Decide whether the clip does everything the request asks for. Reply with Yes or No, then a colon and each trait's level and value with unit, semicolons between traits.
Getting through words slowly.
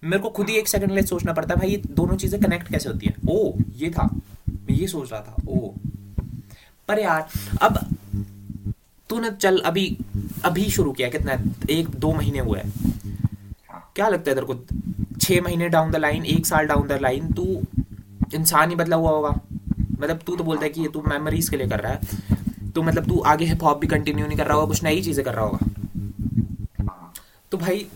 No: average, 130 wpm